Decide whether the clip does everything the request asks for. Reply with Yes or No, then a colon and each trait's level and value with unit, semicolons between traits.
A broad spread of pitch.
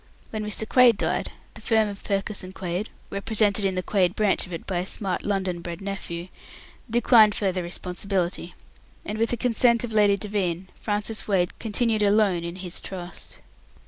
No: average, 2.9 semitones